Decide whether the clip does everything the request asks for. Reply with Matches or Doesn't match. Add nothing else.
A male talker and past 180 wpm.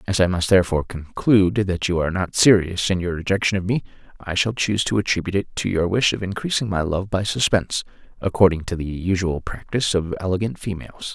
Matches